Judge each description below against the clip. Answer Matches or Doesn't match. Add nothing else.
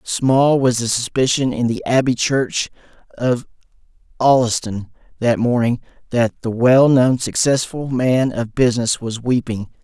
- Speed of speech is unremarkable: Doesn't match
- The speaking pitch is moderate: Doesn't match